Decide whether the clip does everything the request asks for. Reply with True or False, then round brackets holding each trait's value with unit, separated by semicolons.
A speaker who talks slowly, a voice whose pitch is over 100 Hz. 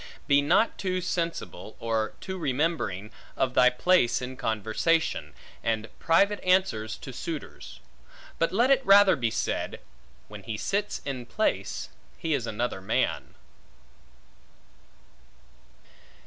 True (120 wpm; 140 Hz)